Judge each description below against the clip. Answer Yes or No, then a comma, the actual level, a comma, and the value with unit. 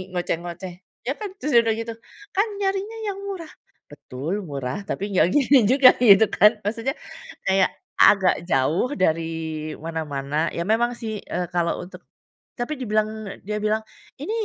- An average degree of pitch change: No, wide, 6.4 semitones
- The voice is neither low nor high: No, high, 205 Hz